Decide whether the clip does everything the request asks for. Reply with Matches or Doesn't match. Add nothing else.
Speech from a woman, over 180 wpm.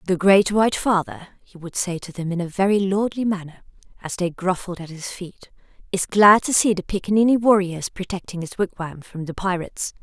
Matches